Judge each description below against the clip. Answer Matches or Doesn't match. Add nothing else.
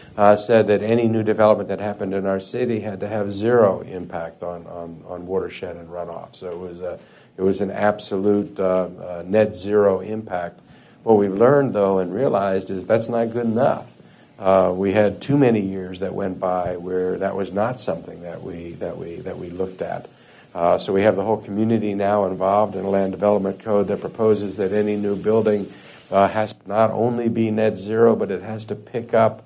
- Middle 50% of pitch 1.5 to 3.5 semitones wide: Matches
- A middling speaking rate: Doesn't match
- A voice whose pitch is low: Matches